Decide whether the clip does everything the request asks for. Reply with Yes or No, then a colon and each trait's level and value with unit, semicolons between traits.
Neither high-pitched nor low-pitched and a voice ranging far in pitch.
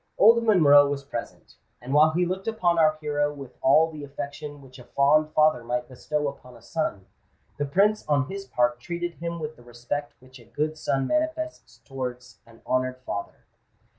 No: medium, 145 Hz; average, 4.1 semitones